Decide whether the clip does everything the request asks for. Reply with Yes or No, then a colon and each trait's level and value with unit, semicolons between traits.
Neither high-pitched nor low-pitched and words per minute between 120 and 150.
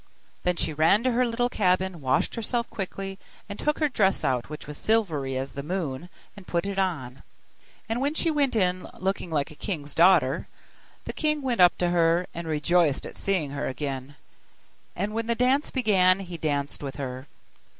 No: medium, 180 Hz; average, 190 wpm